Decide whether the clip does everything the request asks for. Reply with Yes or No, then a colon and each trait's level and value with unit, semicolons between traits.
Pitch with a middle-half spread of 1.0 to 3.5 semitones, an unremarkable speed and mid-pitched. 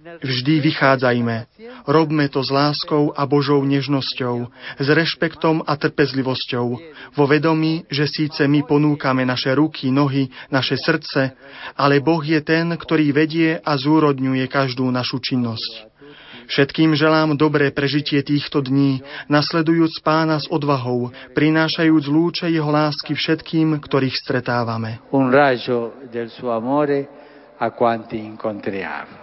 No: average, 2.9 semitones; slow, 105 wpm; medium, 145 Hz